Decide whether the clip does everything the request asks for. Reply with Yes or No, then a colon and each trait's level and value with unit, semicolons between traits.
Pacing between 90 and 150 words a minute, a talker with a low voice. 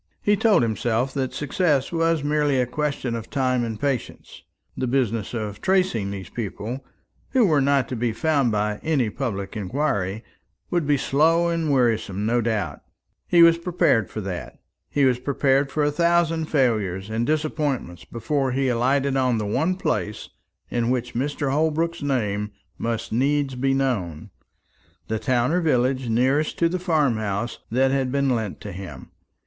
No: average, 165 wpm; low, 130 Hz